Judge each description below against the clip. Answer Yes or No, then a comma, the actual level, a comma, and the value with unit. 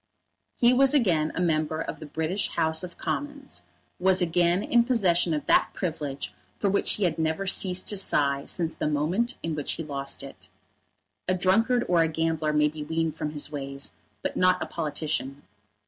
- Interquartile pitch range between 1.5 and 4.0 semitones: Yes, average, 3.7 semitones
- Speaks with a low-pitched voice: No, medium, 165 Hz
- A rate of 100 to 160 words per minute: No, average, 185 wpm